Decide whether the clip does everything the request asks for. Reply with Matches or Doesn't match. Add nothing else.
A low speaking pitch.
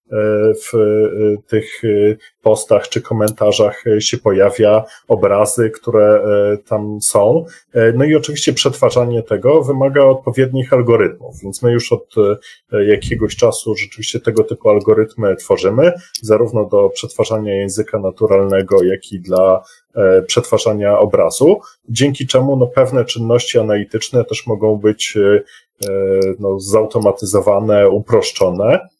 Matches